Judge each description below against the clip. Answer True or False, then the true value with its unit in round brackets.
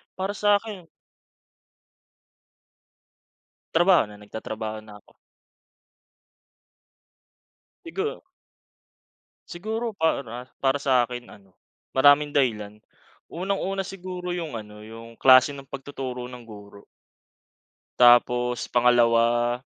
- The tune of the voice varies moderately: False (7.0 semitones)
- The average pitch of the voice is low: True (125 Hz)